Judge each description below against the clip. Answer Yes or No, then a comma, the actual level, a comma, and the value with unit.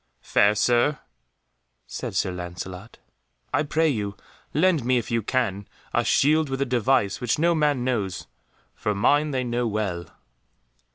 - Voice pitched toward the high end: No, low, 120 Hz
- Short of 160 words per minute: Yes, average, 150 wpm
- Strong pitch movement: Yes, wide, 5.9 semitones